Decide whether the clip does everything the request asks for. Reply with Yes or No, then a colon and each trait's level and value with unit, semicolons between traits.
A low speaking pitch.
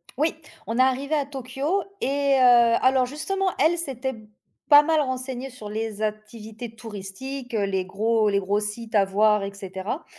No: high, 240 Hz